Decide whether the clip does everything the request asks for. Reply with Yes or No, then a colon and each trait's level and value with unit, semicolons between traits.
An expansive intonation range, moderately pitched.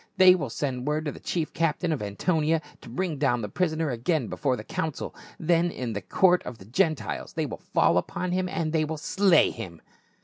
Yes: wide, 5.8 semitones; medium, 155 Hz